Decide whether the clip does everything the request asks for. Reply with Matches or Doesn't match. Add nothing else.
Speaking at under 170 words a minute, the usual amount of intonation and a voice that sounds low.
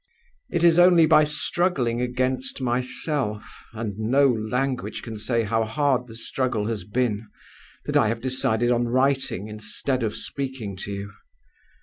Matches